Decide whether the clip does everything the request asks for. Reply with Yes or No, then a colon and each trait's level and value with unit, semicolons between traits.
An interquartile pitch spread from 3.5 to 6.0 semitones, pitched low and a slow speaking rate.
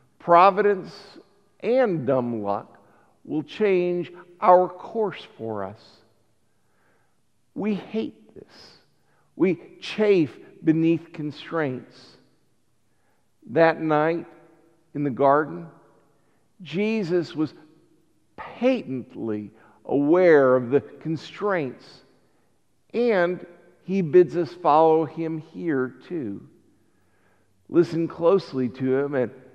No: wide, 5.4 semitones; medium, 160 Hz; slow, 85 wpm